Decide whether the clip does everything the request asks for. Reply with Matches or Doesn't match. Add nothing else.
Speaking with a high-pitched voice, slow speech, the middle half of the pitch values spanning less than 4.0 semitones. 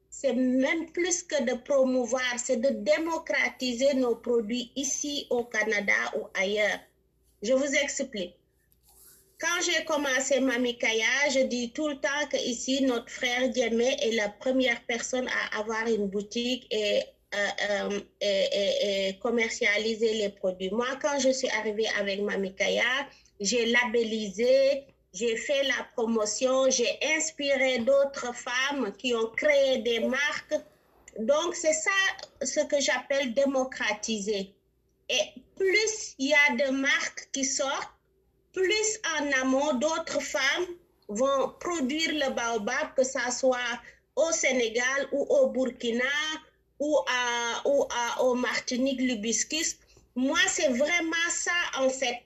Matches